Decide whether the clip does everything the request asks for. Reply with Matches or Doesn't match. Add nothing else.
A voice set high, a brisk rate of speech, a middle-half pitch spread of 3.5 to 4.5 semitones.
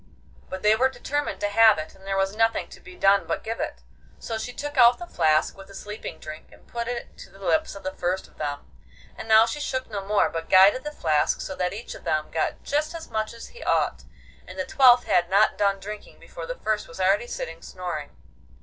Matches